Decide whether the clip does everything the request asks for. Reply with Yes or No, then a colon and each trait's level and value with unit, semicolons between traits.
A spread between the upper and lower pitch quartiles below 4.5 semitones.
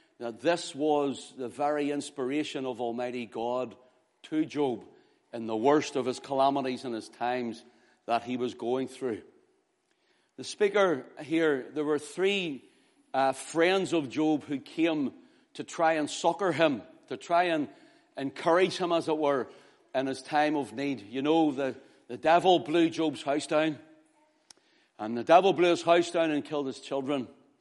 No: average, 4.8 semitones